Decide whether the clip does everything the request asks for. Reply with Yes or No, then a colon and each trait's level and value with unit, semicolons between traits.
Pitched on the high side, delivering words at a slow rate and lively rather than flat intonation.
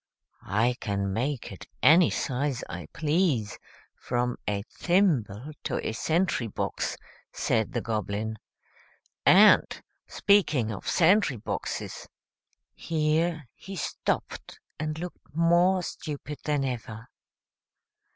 No: medium, 140 Hz; slow, 105 wpm; wide, 6.9 semitones